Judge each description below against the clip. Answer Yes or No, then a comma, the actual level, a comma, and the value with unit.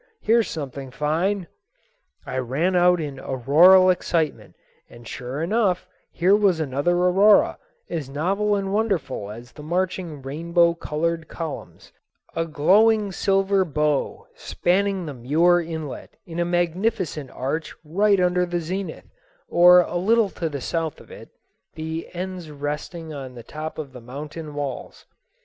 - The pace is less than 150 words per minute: Yes, average, 140 wpm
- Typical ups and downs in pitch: Yes, average, 3.9 semitones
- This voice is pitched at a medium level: Yes, medium, 170 Hz